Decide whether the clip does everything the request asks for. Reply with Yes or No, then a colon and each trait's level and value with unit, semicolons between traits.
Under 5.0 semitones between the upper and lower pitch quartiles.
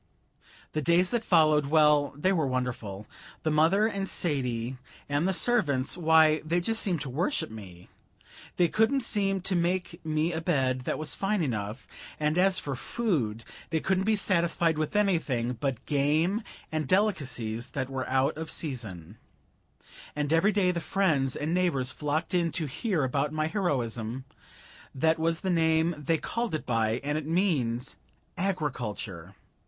No: wide, 5.5 semitones